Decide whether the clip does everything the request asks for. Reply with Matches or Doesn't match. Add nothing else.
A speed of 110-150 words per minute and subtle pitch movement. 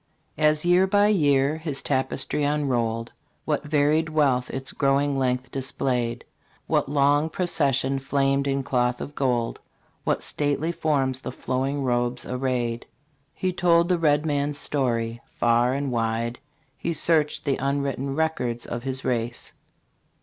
Doesn't match